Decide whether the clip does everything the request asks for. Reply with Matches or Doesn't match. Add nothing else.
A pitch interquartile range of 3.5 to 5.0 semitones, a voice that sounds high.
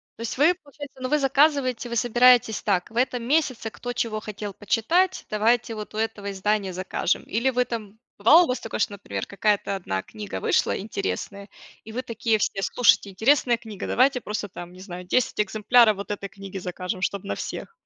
Matches